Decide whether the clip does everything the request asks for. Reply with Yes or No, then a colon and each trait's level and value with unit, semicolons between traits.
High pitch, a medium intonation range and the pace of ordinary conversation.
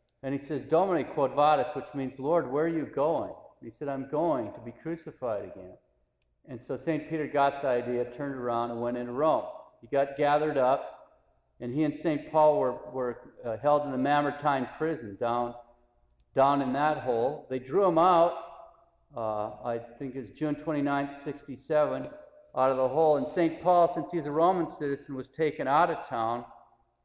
No: medium, 140 Hz; average, 3.9 semitones; average, 185 wpm